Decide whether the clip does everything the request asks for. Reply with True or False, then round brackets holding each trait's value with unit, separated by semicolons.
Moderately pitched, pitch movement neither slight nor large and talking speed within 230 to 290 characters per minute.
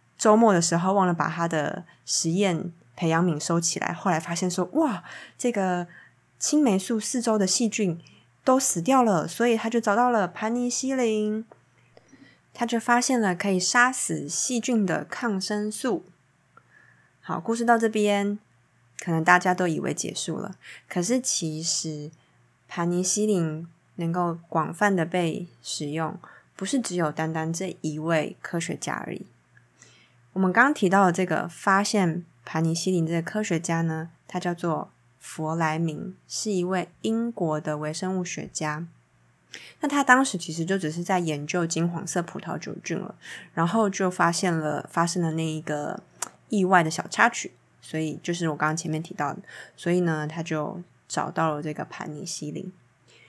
True (175 Hz; 4.4 semitones; 240 characters per minute)